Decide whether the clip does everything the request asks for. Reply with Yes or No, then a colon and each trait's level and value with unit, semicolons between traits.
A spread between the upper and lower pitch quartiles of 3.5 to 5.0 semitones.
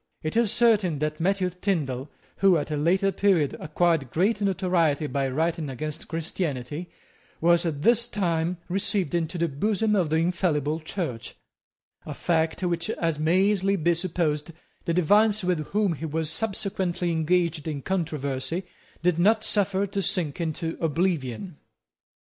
Yes: average, 3.8 semitones